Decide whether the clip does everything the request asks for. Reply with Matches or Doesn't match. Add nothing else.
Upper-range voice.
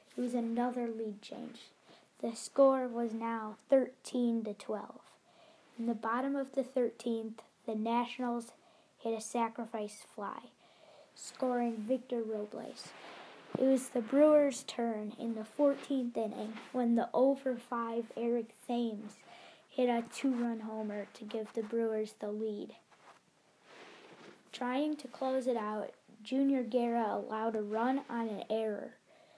Matches